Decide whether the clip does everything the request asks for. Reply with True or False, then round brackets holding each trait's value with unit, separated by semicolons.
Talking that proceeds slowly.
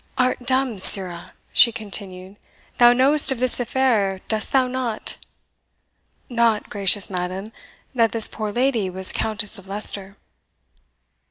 True (125 wpm)